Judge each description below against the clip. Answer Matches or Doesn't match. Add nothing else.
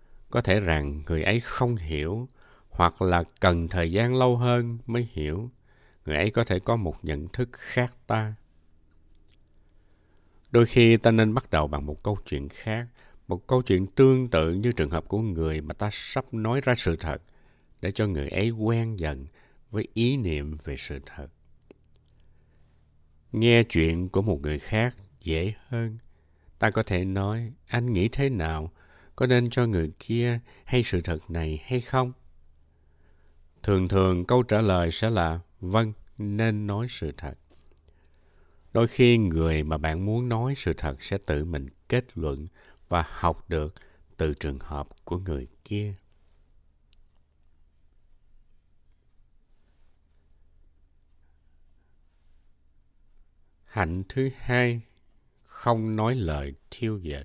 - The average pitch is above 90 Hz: Doesn't match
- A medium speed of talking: Doesn't match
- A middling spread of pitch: Doesn't match